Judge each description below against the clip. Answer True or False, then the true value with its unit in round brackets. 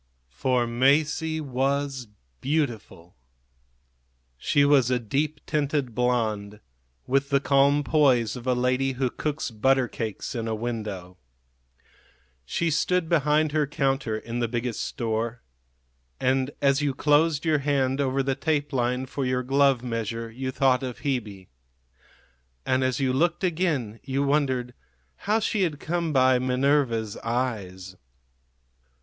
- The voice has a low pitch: True (130 Hz)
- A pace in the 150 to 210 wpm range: False (135 wpm)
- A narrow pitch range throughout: False (3.3 semitones)